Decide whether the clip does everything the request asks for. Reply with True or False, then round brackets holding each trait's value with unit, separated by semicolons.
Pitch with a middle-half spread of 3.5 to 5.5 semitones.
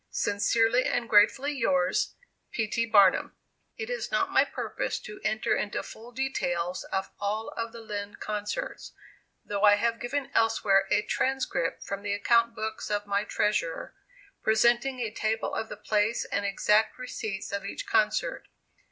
False (2.4 semitones)